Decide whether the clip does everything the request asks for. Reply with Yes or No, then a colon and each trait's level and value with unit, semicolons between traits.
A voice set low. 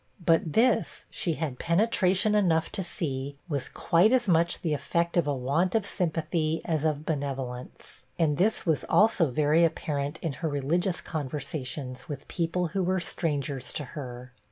No: medium, 160 Hz